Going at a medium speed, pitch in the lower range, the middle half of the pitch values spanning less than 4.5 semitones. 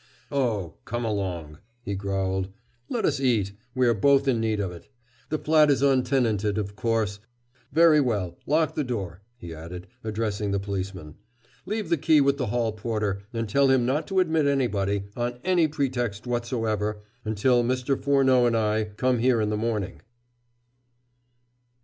No: average, 160 wpm; low, 115 Hz; average, 4.9 semitones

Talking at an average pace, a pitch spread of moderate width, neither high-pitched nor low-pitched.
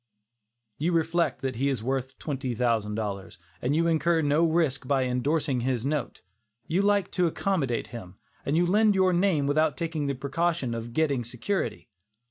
Yes: average, 170 wpm; average, 5.0 semitones; medium, 145 Hz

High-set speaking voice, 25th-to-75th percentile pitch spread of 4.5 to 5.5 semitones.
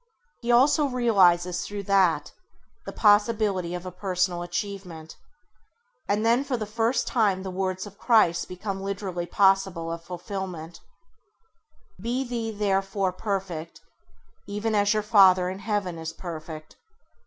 No: high, 195 Hz; average, 3.0 semitones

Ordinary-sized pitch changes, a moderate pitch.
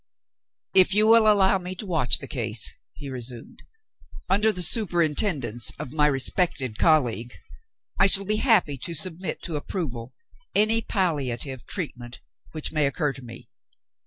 No: wide, 6.5 semitones; medium, 160 Hz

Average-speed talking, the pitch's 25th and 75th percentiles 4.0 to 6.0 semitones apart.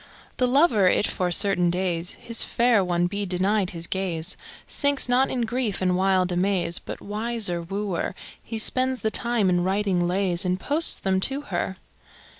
Yes: average, 170 wpm; average, 4.4 semitones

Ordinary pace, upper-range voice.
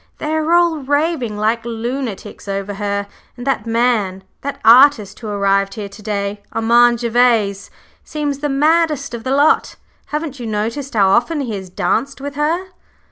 Yes: average, 165 wpm; high, 235 Hz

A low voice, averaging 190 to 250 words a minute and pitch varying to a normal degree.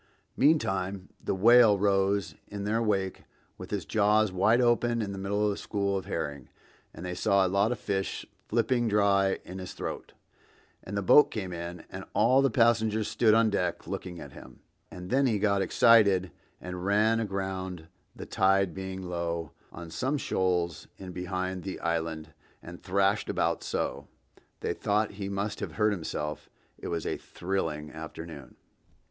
No: very low, 95 Hz; average, 170 wpm; average, 3.0 semitones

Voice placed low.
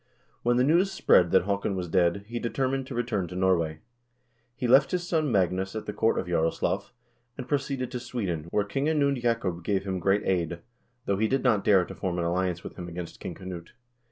Yes: low, 100 Hz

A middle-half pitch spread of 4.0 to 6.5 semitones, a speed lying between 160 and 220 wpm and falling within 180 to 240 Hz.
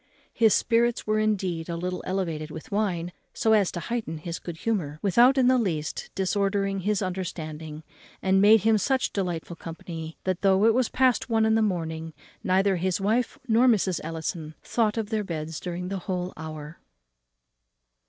Yes: average, 4.7 semitones; average, 175 wpm; high, 190 Hz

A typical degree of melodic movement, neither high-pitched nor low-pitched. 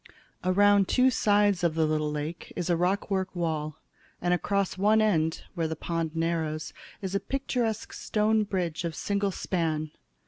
Yes: average, 4.0 semitones; medium, 180 Hz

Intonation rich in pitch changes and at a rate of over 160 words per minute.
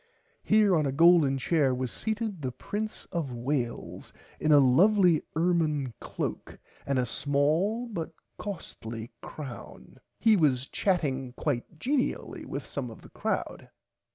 No: wide, 6.1 semitones; slow, 135 wpm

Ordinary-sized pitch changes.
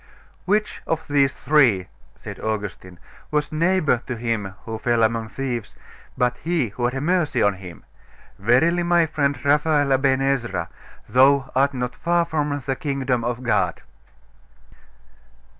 Yes: average, 4.4 semitones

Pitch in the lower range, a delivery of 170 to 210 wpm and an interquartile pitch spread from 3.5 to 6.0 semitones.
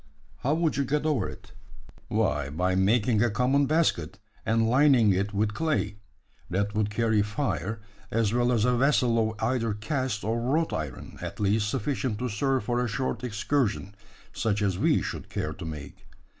Yes: low, 115 Hz; average, 175 wpm; average, 3.9 semitones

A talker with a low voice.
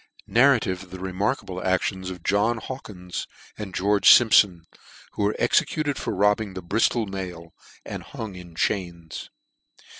Yes: very low, 95 Hz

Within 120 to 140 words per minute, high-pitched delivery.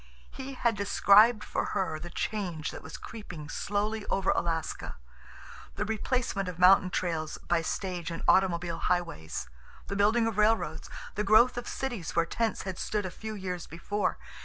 No: average, 160 wpm; high, 195 Hz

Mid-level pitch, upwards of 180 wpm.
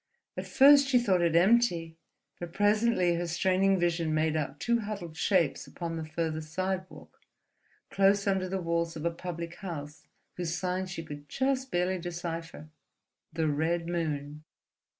No: medium, 175 Hz; average, 150 wpm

